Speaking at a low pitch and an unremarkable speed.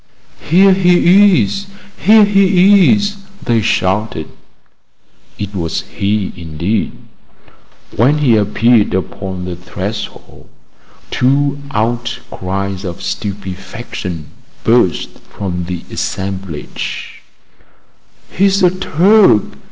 No: low, 110 Hz; slow, 90 wpm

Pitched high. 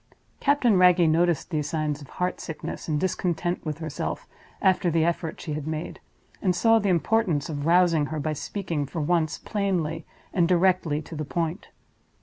No: medium, 165 Hz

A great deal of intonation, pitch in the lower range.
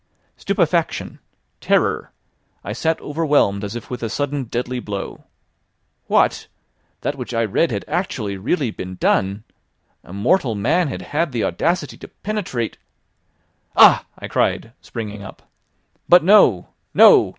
Yes: wide, 6.9 semitones; low, 120 Hz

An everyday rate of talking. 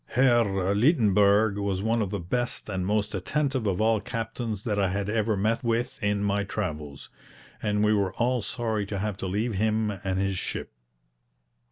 Yes: average, 180 wpm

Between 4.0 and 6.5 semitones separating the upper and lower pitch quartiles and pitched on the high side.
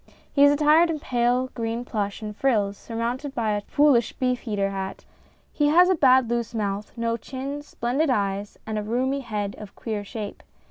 Yes: average, 4.4 semitones; high, 235 Hz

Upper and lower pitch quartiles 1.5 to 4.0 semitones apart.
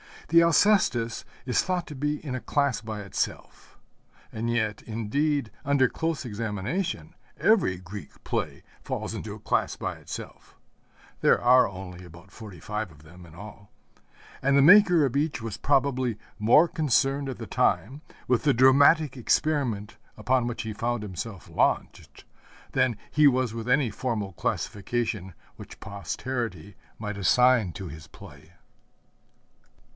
No: wide, 5.4 semitones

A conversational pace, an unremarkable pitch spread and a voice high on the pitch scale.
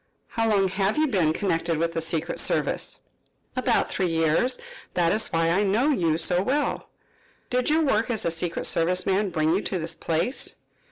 No: average, 185 wpm; average, 4.7 semitones; medium, 180 Hz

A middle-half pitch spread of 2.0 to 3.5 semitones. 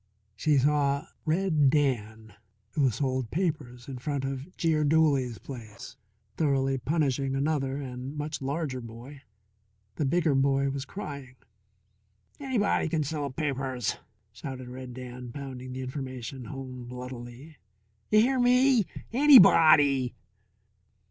Yes: average, 3.1 semitones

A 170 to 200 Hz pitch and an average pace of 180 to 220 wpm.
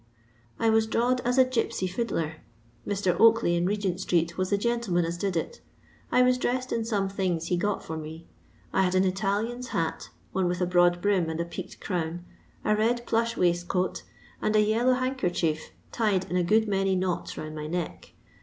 Yes: high, 190 Hz; average, 190 wpm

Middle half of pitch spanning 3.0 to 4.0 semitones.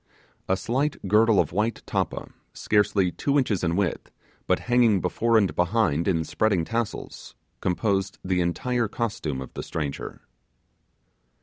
No: average, 4.5 semitones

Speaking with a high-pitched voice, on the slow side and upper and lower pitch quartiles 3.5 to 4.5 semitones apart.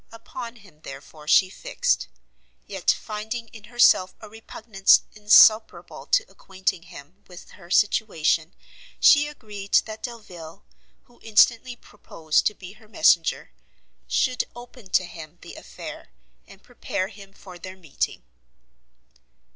Yes: high, 205 Hz; slow, 125 wpm; average, 4.0 semitones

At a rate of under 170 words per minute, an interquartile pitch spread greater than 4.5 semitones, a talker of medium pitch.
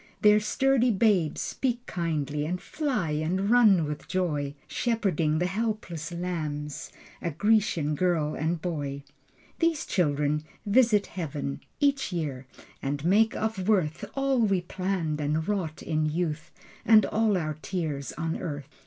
Yes: slow, 135 wpm; wide, 5.6 semitones; medium, 175 Hz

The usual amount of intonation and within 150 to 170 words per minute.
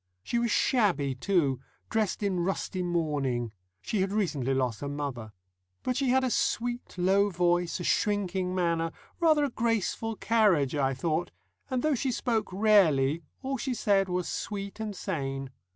No: wide, 6.9 semitones; average, 160 wpm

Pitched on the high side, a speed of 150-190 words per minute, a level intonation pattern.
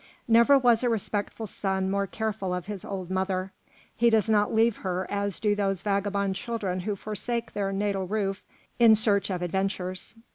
Yes: high, 200 Hz; average, 175 wpm; narrow, 2.3 semitones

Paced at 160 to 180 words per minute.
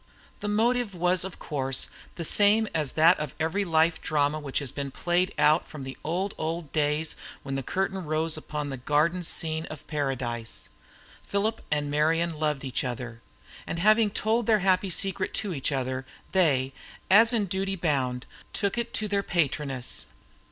Yes: average, 170 wpm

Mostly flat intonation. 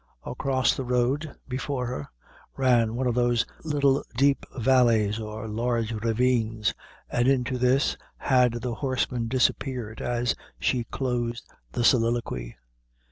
Yes: narrow, 2.2 semitones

